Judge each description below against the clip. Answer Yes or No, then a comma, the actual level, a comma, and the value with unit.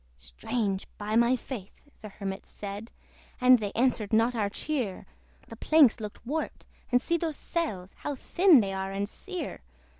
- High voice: Yes, high, 225 Hz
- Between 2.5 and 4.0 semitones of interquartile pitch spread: No, average, 5.1 semitones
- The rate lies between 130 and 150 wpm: No, average, 160 wpm